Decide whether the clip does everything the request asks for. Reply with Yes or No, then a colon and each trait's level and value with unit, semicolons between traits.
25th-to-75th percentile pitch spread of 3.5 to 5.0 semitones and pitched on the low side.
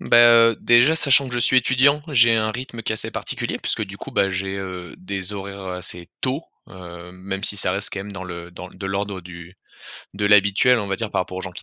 Yes: average, 4.0 semitones; low, 100 Hz